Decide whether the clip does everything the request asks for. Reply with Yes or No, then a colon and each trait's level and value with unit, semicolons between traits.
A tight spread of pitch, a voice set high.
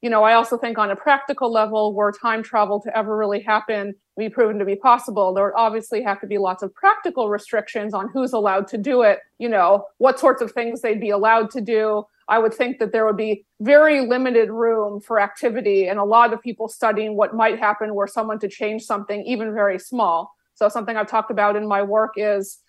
Yes: narrow, 2.2 semitones; high, 220 Hz